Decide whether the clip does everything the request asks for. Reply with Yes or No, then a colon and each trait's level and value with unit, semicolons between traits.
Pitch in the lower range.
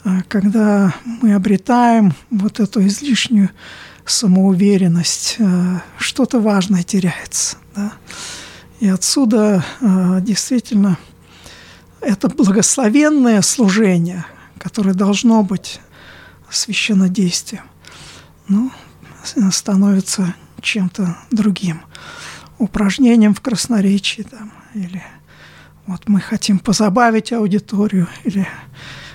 No: high, 200 Hz